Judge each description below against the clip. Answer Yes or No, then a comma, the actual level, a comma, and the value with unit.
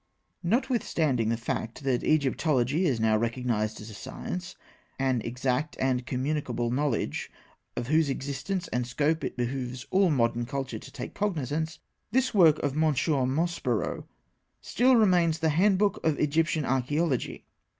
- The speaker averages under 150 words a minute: Yes, average, 140 wpm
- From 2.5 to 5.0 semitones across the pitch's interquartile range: Yes, average, 4.7 semitones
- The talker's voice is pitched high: No, medium, 140 Hz